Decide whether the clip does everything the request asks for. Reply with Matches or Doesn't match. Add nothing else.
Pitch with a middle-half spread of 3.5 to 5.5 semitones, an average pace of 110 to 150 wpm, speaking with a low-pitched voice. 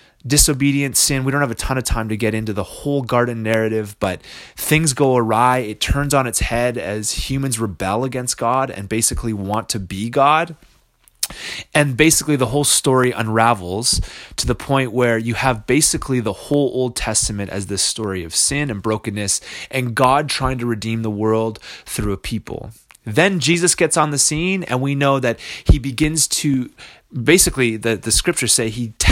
Doesn't match